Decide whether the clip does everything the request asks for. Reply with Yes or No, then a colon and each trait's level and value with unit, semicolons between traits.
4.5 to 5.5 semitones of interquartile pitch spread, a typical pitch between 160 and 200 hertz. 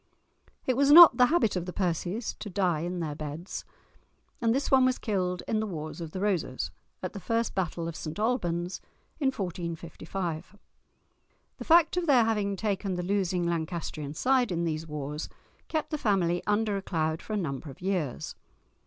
Yes: average, 4.9 semitones; medium, 185 Hz